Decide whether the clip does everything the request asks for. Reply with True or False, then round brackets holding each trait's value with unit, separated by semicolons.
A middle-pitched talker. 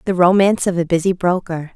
True (180 Hz)